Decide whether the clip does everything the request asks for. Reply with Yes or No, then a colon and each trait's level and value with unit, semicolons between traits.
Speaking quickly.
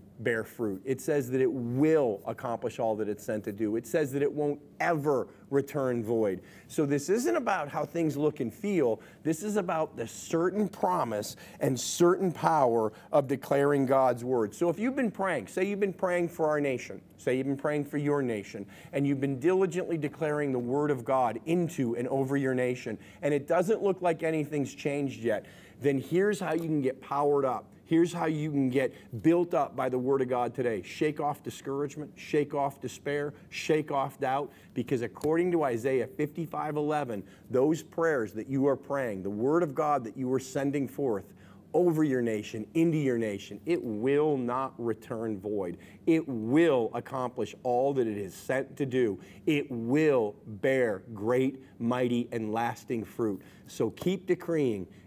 No: average, 180 wpm